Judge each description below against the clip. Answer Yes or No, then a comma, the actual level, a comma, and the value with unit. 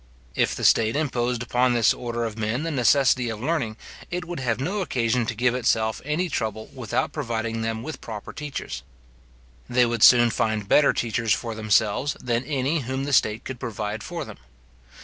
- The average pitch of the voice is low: Yes, low, 120 Hz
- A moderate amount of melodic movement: Yes, average, 3.4 semitones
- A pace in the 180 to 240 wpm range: Yes, average, 185 wpm